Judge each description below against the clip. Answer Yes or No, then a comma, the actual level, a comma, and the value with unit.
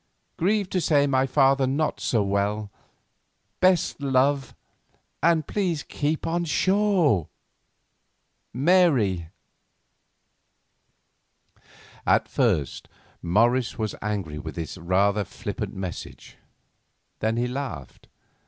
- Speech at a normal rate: No, slow, 95 wpm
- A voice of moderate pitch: No, low, 130 Hz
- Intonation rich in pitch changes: Yes, wide, 7.6 semitones